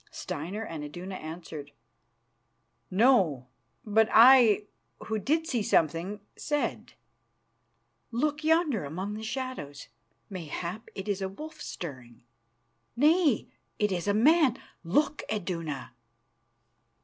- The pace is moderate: No, slow, 105 wpm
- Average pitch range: No, wide, 7.6 semitones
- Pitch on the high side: Yes, high, 205 Hz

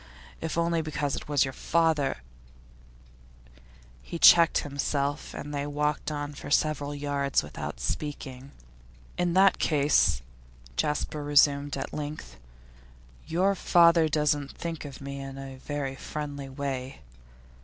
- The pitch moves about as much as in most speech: No, narrow, 2.1 semitones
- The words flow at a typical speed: No, slow, 130 wpm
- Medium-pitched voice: Yes, medium, 145 Hz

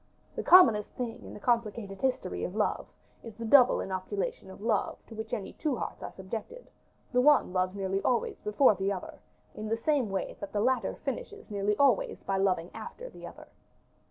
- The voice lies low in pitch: No, high, 215 Hz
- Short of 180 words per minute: No, average, 190 wpm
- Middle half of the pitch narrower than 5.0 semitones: Yes, average, 4.2 semitones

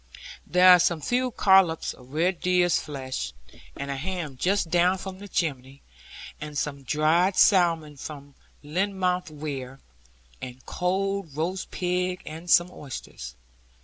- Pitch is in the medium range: Yes, medium, 170 Hz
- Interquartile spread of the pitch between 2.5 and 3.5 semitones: No, average, 4.3 semitones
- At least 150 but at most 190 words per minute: No, slow, 135 wpm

